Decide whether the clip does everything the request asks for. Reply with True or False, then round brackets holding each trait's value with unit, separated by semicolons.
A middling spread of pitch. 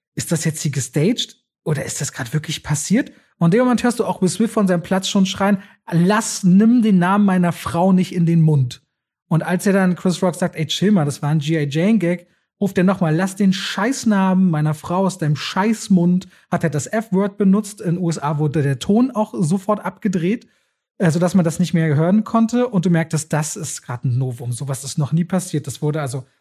True (4.3 semitones)